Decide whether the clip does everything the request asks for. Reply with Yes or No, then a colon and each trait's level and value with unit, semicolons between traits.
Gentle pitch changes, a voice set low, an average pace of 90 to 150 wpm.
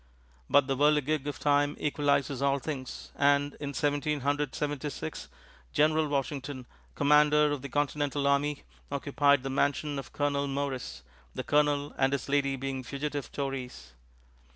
No: narrow, 1.2 semitones; medium, 145 Hz; average, 145 wpm